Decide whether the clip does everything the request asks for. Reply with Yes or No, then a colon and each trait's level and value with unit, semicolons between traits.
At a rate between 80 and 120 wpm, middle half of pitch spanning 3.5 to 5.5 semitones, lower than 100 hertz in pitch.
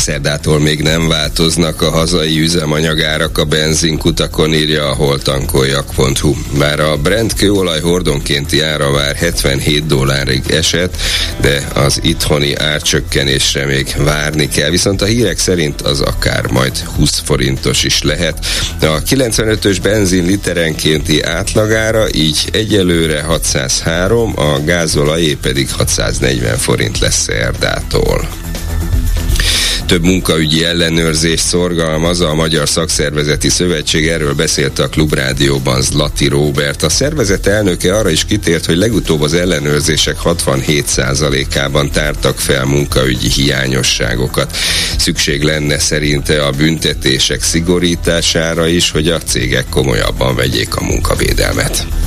No: average, 115 wpm; average, 2.7 semitones; very low, 80 Hz